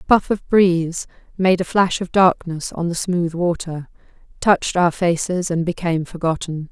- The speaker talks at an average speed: Yes, average, 170 wpm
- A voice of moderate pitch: Yes, medium, 175 Hz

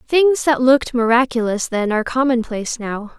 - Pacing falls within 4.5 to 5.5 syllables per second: Yes, 5.4 syllables/s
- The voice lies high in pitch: Yes, high, 245 Hz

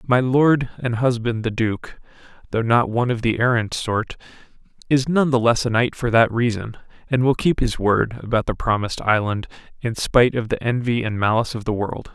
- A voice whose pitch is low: Yes, low, 120 Hz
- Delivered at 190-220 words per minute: Yes, fast, 205 wpm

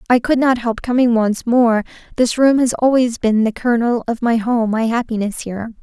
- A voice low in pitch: No, high, 235 Hz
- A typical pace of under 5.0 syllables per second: No, 5.1 syllables/s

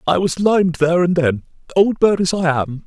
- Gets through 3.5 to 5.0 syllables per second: No, 5.4 syllables/s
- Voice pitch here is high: No, medium, 170 Hz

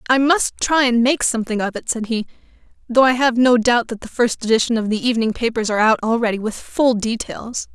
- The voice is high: Yes, high, 235 Hz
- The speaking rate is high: Yes, fast, 225 wpm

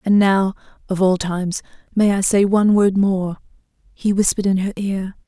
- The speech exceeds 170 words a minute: No, average, 160 wpm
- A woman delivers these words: Yes, female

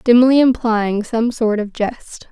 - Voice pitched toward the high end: Yes, high, 230 Hz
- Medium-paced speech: Yes, average, 155 wpm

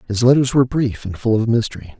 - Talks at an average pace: No, fast, 240 wpm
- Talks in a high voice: No, low, 115 Hz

